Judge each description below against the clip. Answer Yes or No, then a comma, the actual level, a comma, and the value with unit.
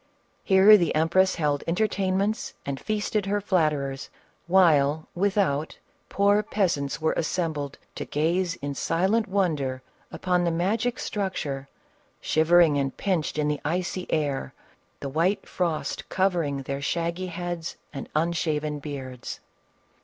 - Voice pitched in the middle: Yes, medium, 170 Hz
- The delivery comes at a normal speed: No, slow, 125 wpm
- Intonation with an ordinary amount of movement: Yes, average, 4.4 semitones